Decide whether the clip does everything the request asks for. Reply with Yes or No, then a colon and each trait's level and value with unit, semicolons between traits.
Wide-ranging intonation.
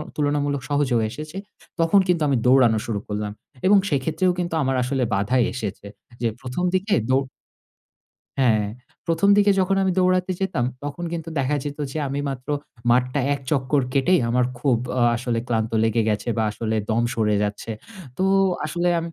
Yes: wide, 6.0 semitones